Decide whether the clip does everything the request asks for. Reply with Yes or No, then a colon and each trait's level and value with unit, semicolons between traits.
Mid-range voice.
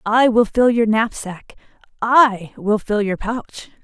No: high, 220 Hz